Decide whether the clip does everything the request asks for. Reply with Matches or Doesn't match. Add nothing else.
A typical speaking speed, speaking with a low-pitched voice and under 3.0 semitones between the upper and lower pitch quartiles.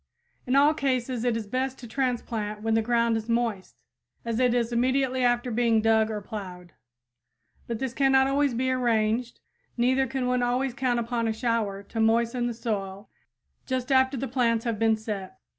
Doesn't match